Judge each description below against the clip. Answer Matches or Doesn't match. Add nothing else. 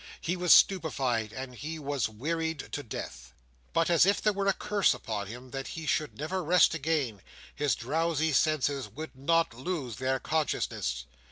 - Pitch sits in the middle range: Matches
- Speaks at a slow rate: Doesn't match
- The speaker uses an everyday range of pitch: Matches